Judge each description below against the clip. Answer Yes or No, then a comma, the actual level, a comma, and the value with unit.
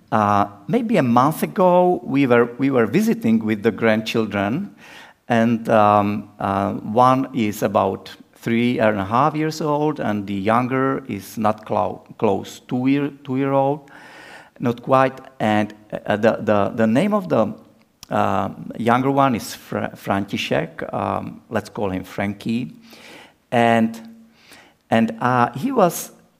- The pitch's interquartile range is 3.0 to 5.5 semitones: Yes, average, 4.3 semitones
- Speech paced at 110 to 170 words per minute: Yes, average, 145 wpm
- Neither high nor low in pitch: No, low, 120 Hz